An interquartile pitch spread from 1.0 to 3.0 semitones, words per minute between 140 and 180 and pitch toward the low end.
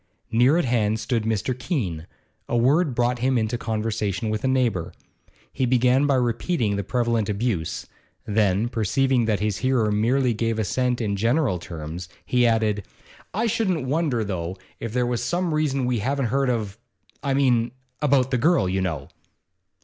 No: average, 3.7 semitones; average, 165 wpm; low, 120 Hz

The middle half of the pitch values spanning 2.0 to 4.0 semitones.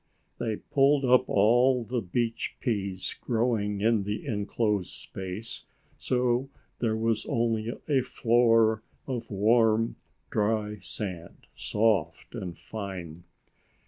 Yes: narrow, 2.6 semitones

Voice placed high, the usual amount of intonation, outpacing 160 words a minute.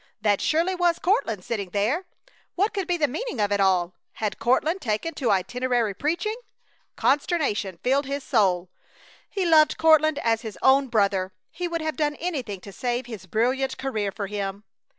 No: very high, 250 Hz; wide, 7.4 semitones; average, 170 wpm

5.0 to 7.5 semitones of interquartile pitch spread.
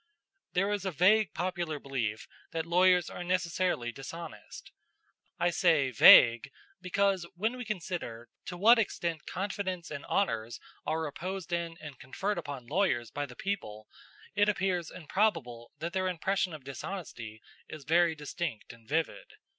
Yes: average, 5.3 semitones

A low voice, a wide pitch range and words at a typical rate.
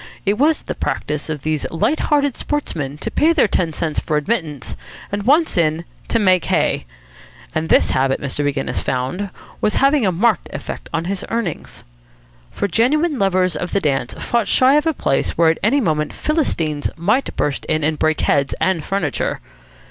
No: medium, 180 Hz; wide, 7.5 semitones; average, 180 wpm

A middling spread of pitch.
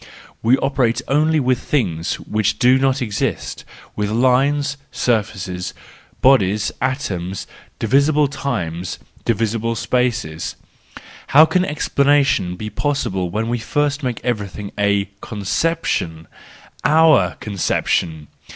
No: wide, 5.7 semitones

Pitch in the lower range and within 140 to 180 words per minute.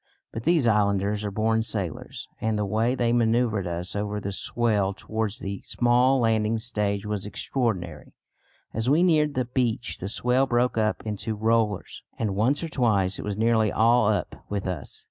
Yes: low, 110 Hz; average, 175 wpm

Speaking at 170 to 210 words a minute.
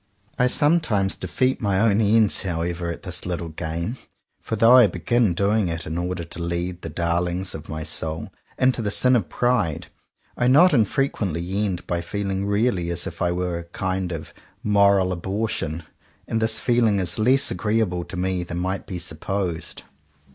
Yes: average, 175 wpm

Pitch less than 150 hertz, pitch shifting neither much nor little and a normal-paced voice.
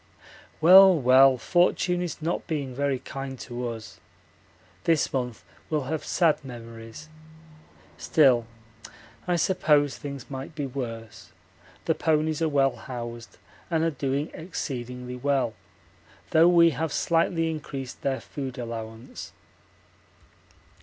No: medium, 140 Hz; average, 4.3 semitones; slow, 120 wpm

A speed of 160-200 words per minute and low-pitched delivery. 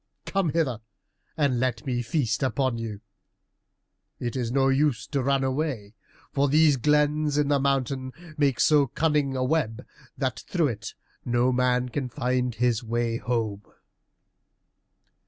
No: average, 145 wpm; low, 130 Hz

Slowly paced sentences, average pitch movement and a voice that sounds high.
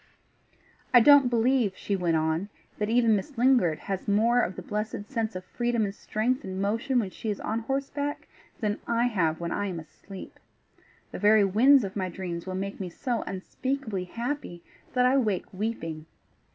No: average, 180 wpm; average, 4.5 semitones; high, 210 Hz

